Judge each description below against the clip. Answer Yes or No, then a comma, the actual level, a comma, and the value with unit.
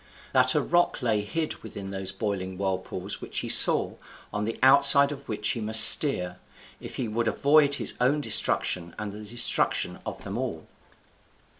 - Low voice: Yes, low, 110 Hz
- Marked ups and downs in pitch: Yes, wide, 5.8 semitones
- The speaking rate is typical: Yes, average, 170 wpm